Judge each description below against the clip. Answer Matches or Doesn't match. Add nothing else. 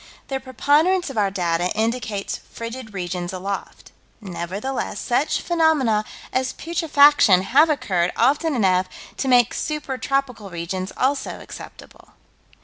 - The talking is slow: Matches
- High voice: Matches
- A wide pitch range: Matches